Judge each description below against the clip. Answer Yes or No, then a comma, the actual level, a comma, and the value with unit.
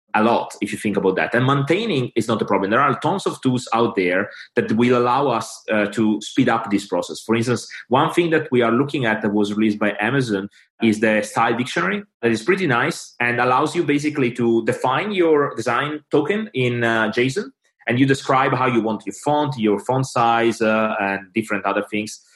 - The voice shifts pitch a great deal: No, average, 4.2 semitones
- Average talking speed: No, fast, 215 wpm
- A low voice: Yes, low, 120 Hz